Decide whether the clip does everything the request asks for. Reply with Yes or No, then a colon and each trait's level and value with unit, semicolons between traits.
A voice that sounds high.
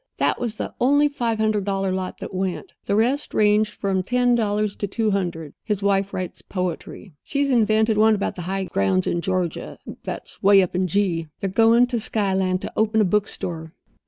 Yes: high, 200 Hz